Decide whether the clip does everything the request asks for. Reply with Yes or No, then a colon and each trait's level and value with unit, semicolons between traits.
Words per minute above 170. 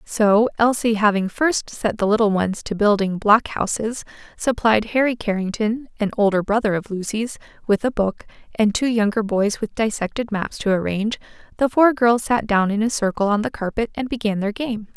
Yes: average, 180 wpm